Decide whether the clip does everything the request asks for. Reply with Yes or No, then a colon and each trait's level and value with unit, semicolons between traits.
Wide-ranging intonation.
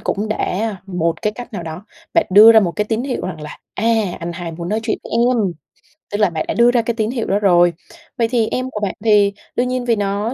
No: average, 4.0 semitones